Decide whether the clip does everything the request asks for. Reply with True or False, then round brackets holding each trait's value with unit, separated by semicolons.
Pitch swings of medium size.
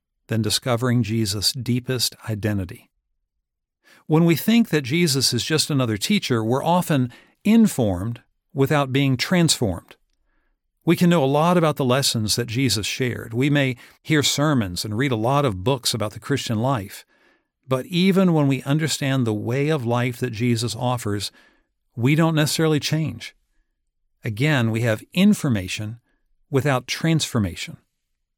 True (4.8 semitones)